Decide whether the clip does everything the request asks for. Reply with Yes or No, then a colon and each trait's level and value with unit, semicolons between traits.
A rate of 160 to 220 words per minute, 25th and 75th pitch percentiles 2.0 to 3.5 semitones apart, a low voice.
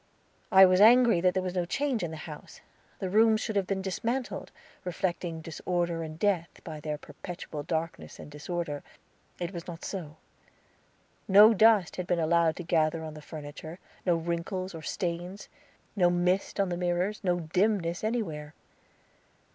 No: average, 165 wpm; average, 2.9 semitones; medium, 175 Hz